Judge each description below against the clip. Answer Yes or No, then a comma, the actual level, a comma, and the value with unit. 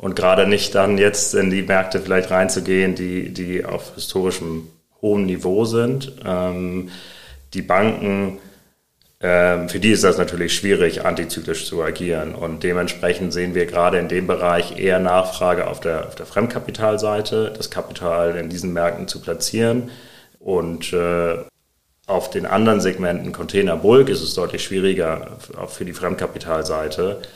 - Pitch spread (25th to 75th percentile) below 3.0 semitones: Yes, narrow, 2.4 semitones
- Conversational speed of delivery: Yes, average, 150 wpm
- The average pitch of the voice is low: Yes, very low, 90 Hz